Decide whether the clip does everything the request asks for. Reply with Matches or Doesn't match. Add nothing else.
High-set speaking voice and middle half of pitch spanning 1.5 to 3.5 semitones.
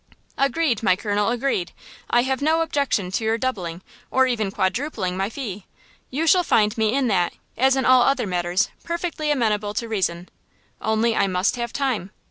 Doesn't match